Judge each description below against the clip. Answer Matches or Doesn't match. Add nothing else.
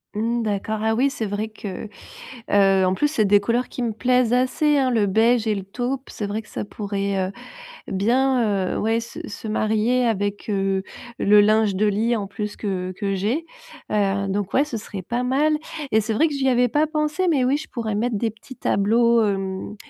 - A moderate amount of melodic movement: Matches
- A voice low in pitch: Doesn't match